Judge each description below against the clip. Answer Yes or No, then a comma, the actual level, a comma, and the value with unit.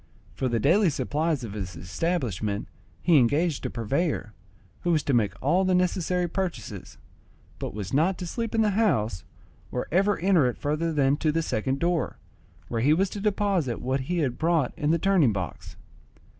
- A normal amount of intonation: No, wide, 6.8 semitones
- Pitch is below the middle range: No, medium, 155 Hz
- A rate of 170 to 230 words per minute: Yes, average, 185 wpm